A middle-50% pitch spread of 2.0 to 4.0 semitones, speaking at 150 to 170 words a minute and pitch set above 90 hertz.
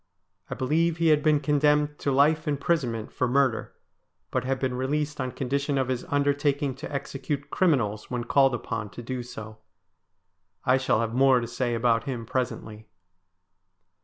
Yes: average, 3.1 semitones; average, 160 wpm; low, 135 Hz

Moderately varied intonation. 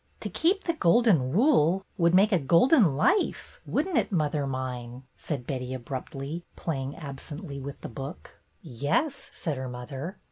No: wide, 6.4 semitones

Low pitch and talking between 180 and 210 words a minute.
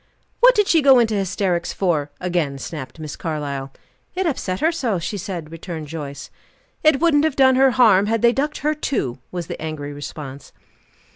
No: medium, 185 Hz; average, 185 wpm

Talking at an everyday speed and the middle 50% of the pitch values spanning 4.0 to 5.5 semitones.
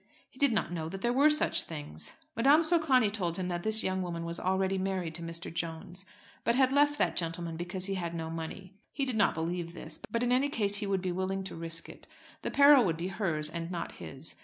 No: fast, 235 wpm; average, 5.1 semitones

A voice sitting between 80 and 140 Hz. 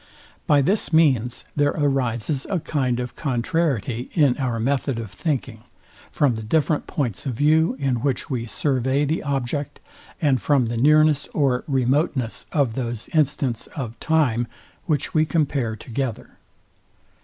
Yes: low, 135 Hz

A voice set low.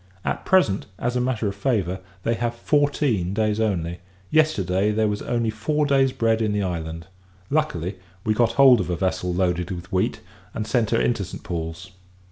Yes: low, 105 Hz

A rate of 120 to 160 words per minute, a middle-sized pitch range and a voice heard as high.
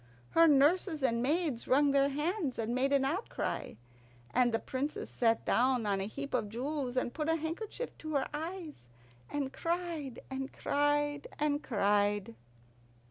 Yes: average, 155 wpm; average, 3.9 semitones; very high, 280 Hz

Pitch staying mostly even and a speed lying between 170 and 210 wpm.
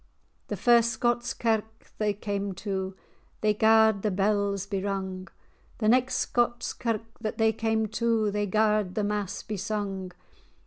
No: narrow, 2.0 semitones; average, 155 wpm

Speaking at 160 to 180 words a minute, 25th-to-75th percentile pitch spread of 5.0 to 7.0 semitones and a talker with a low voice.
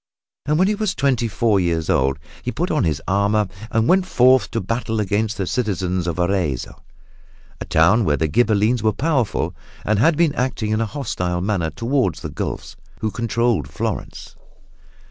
Yes: average, 175 wpm; wide, 5.4 semitones; low, 110 Hz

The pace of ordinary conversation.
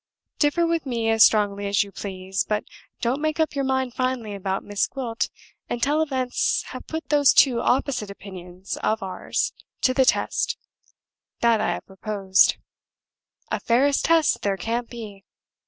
Yes: average, 155 wpm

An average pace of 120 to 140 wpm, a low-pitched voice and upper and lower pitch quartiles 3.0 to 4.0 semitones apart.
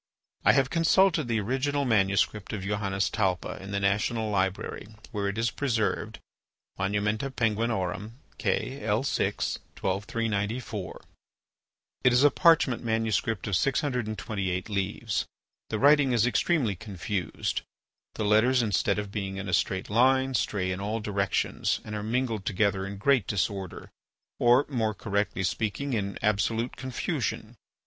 Yes: slow, 135 wpm; low, 110 Hz; average, 3.7 semitones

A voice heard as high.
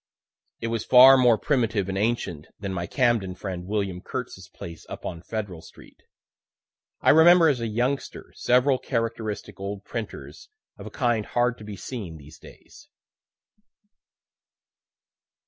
No: low, 110 Hz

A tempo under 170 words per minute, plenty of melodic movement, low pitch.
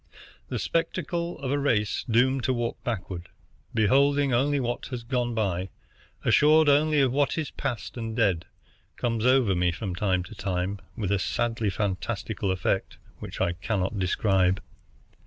Yes: average, 155 wpm; wide, 5.7 semitones; low, 115 Hz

